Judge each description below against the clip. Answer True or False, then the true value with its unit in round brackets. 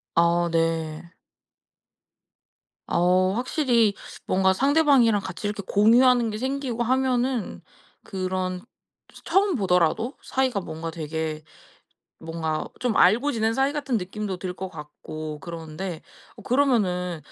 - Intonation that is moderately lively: False (6.5 semitones)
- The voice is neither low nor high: False (195 Hz)